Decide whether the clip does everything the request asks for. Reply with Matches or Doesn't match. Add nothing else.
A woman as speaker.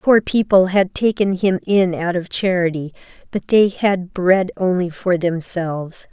Matches